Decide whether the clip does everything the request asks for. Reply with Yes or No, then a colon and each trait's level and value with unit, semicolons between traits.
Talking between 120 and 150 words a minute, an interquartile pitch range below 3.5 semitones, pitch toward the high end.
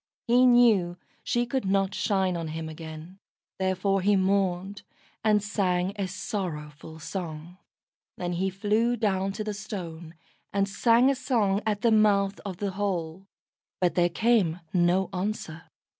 Yes: average, 145 wpm; average, 3.0 semitones; high, 195 Hz